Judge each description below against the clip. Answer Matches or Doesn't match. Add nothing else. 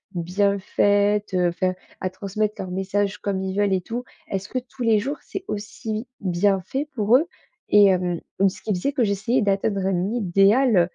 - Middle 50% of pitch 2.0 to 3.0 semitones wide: Matches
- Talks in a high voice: Matches